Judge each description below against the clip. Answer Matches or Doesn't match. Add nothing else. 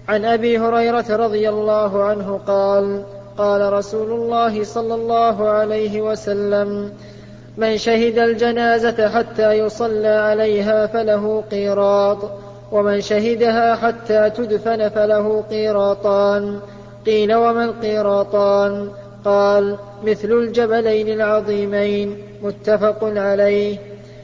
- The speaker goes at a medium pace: Matches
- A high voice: Matches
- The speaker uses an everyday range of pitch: Doesn't match